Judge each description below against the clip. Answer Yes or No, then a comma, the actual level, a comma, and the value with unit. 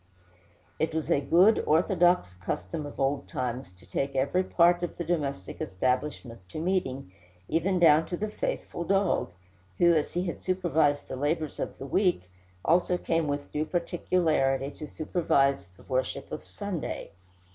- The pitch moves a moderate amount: Yes, average, 4.4 semitones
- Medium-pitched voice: Yes, medium, 155 Hz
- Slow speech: No, average, 155 wpm